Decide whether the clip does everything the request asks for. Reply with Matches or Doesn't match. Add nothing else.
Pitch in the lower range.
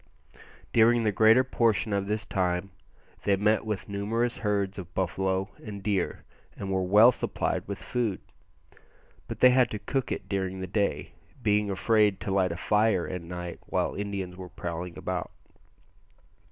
Matches